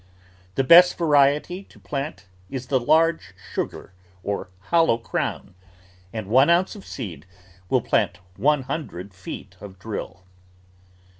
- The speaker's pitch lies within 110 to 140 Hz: Yes, low, 135 Hz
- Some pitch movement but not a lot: No, wide, 8.0 semitones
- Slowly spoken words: Yes, slow, 130 wpm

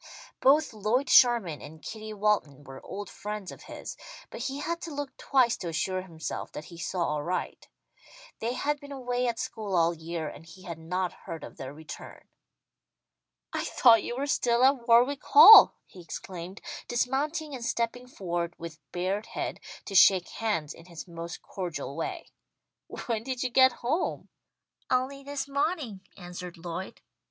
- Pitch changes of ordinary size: No, wide, 7.2 semitones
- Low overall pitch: No, high, 210 Hz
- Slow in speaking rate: No, average, 165 wpm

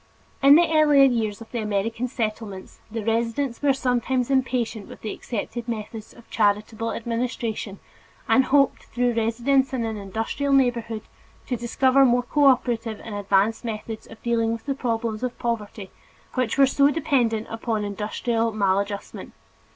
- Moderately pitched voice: No, high, 230 Hz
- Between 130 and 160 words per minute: Yes, average, 150 wpm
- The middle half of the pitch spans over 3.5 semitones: No, average, 2.8 semitones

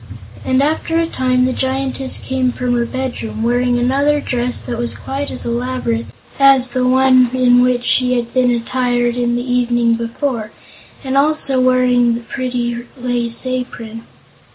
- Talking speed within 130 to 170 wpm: Yes, average, 155 wpm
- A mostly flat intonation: Yes, narrow, 1.4 semitones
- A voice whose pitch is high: Yes, very high, 250 Hz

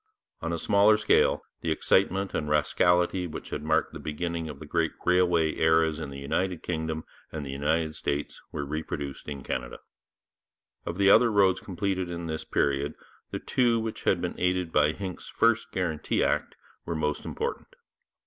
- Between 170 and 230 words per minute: Yes, average, 175 wpm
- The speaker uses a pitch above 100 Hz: No, very low, 80 Hz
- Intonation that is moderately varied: Yes, average, 3.4 semitones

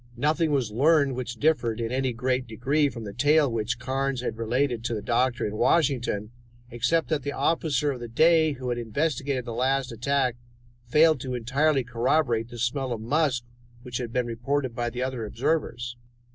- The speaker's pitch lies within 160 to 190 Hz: No, low, 125 Hz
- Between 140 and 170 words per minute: No, average, 185 wpm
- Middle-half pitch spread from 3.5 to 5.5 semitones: No, average, 3.1 semitones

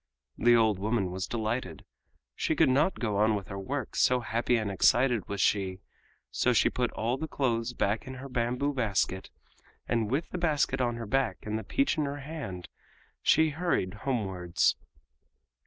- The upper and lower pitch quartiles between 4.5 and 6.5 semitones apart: Yes, average, 4.8 semitones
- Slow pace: No, average, 175 wpm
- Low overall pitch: Yes, low, 115 Hz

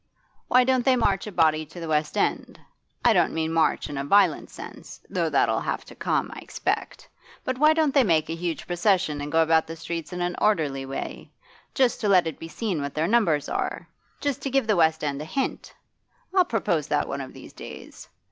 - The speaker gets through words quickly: Yes, fast, 225 wpm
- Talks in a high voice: No, medium, 165 Hz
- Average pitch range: No, wide, 6.2 semitones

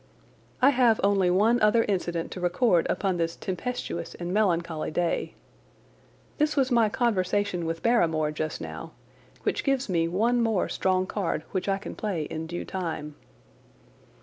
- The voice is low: No, medium, 185 Hz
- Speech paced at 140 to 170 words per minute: Yes, average, 150 wpm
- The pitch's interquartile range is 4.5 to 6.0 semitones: Yes, average, 4.9 semitones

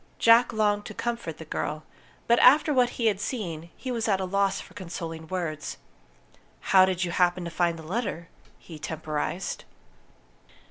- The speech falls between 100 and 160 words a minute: No, average, 170 wpm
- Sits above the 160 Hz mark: Yes, medium, 185 Hz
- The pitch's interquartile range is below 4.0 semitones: No, average, 5.0 semitones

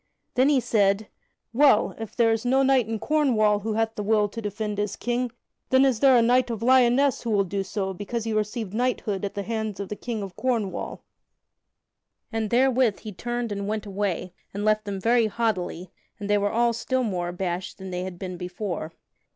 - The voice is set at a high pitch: Yes, high, 215 Hz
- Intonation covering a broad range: No, average, 3.2 semitones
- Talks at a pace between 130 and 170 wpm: No, fast, 205 wpm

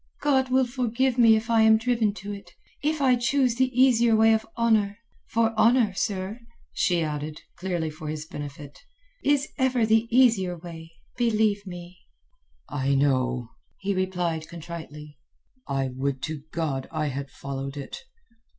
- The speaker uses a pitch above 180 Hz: Yes, high, 190 Hz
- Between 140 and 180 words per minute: Yes, average, 150 wpm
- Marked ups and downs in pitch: Yes, wide, 7.3 semitones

